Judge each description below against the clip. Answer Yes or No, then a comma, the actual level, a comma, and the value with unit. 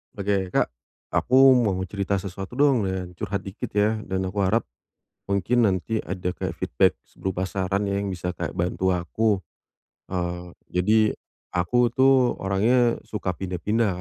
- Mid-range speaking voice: No, low, 100 Hz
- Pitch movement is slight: No, average, 3.2 semitones